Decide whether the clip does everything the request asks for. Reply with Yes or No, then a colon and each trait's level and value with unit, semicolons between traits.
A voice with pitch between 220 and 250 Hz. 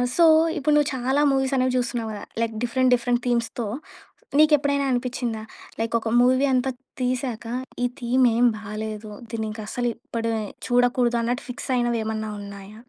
Yes: high, 245 Hz